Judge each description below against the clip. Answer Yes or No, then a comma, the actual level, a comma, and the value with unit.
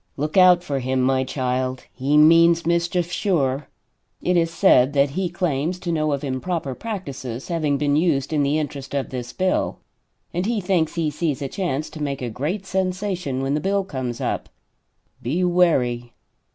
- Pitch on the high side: No, medium, 150 Hz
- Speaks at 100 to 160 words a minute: No, average, 180 wpm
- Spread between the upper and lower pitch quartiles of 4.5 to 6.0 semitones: Yes, average, 4.9 semitones